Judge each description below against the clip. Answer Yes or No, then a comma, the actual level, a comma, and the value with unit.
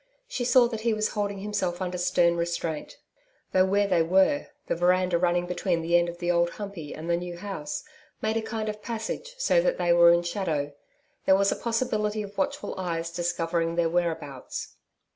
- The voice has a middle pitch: Yes, medium, 180 Hz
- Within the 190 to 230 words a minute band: Yes, average, 195 wpm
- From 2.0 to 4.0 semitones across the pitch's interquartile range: Yes, average, 3.6 semitones